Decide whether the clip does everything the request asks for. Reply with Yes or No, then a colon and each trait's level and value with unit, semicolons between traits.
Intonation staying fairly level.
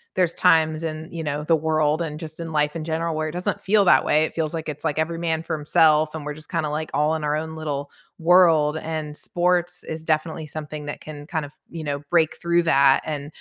Yes: narrow, 1.6 semitones